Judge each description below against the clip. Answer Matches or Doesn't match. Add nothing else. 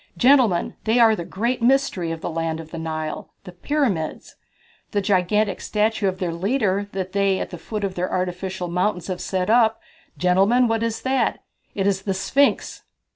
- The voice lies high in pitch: Matches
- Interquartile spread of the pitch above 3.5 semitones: Matches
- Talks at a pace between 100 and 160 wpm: Doesn't match